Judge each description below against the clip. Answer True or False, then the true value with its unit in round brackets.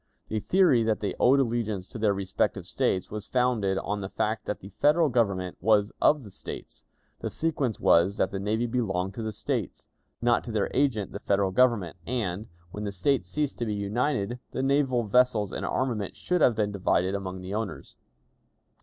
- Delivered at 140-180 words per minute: False (190 wpm)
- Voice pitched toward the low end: True (110 Hz)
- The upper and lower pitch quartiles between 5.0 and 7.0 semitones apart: False (4.0 semitones)